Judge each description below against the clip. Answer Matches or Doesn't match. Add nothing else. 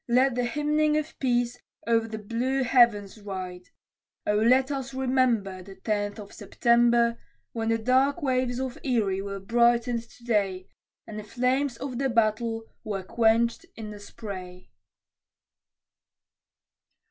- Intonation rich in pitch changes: Doesn't match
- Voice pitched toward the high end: Matches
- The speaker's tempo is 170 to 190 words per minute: Doesn't match